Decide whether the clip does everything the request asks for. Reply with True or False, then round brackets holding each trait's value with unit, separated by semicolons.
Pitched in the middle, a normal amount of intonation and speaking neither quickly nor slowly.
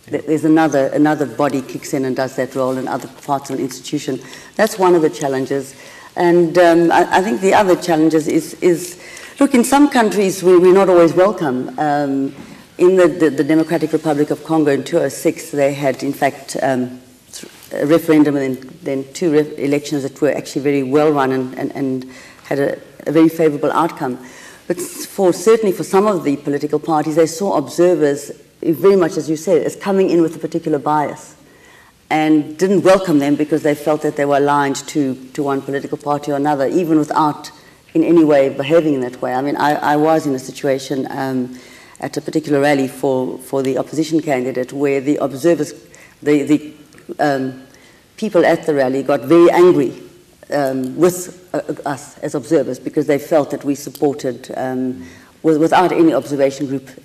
True (150 Hz; 3.1 semitones; 185 wpm)